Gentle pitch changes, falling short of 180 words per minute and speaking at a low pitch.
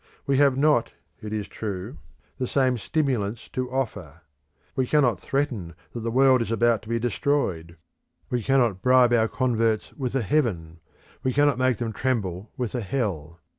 No: average, 4.0 semitones; average, 170 wpm; low, 120 Hz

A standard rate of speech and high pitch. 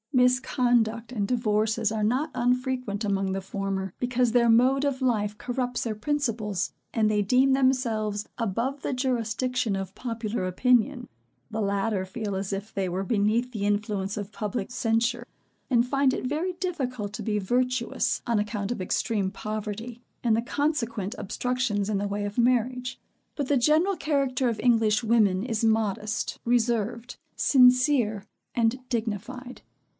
Yes: average, 150 wpm; high, 230 Hz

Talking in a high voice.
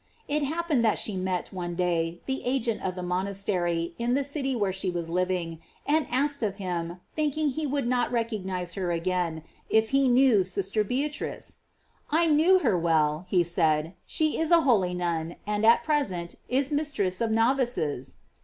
Yes: high, 200 Hz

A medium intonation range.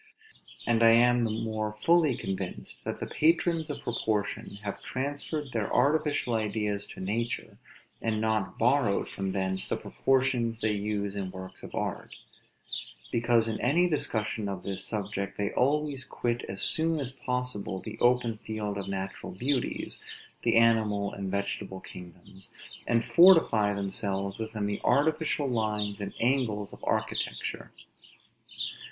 Yes: average, 3.8 semitones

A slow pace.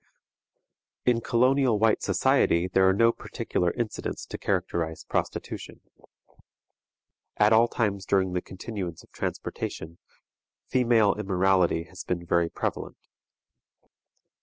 Yes: slow, 110 wpm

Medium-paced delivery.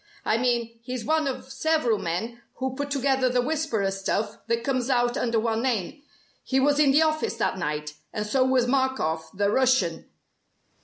Yes: average, 175 wpm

